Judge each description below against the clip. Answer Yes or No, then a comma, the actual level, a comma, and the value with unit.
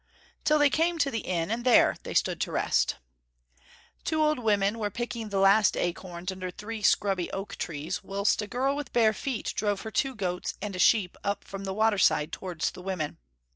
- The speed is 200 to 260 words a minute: Yes, fast, 205 wpm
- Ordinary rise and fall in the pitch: Yes, average, 3.8 semitones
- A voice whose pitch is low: No, high, 205 Hz